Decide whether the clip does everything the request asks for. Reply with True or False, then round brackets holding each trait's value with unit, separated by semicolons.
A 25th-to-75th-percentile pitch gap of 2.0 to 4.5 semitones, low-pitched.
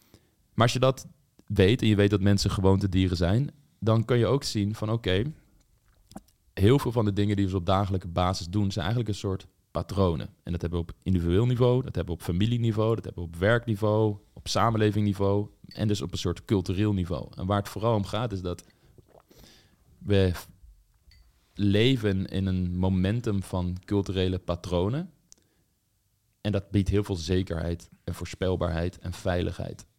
True (2.9 semitones; 100 Hz)